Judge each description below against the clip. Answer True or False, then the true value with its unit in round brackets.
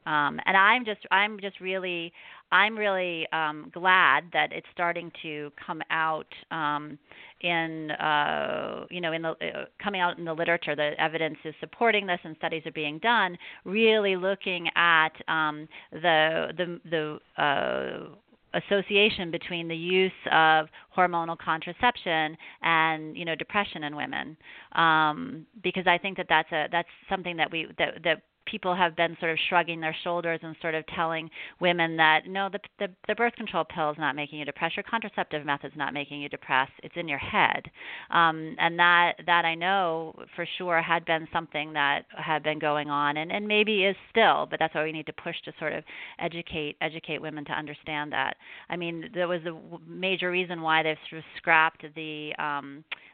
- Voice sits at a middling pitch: True (165 Hz)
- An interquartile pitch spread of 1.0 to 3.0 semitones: True (2.5 semitones)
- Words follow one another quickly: False (185 wpm)